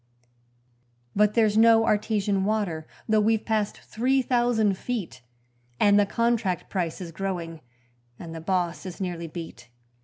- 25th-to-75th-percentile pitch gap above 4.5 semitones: No, average, 4.2 semitones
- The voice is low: No, high, 205 Hz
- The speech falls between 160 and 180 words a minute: No, average, 140 wpm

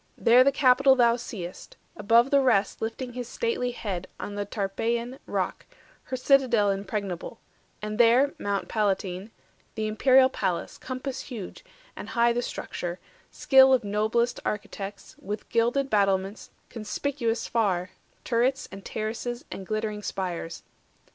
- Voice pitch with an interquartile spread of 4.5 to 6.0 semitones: No, average, 3.7 semitones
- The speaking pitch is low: No, high, 225 Hz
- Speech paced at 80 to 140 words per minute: Yes, slow, 135 wpm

